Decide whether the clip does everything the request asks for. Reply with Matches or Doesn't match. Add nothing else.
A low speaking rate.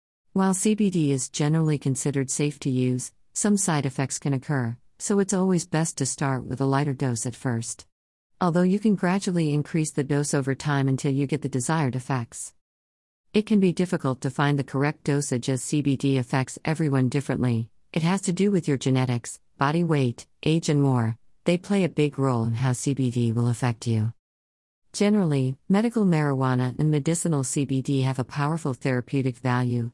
Doesn't match